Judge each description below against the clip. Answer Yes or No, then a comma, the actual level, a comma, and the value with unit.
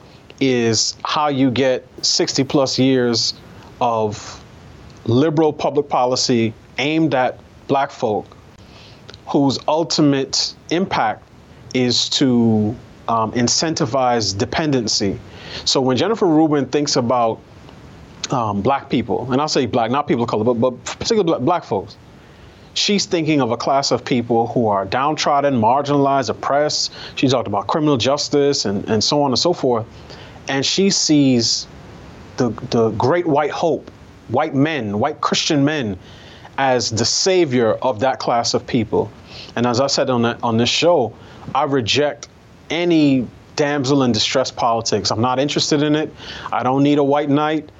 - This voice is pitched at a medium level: No, low, 130 Hz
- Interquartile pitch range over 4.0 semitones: No, average, 3.7 semitones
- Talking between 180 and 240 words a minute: No, average, 145 wpm